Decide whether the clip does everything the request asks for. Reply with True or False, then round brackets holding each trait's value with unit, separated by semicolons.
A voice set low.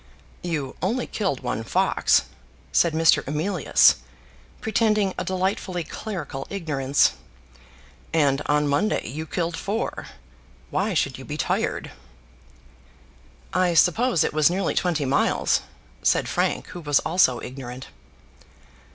False (165 Hz)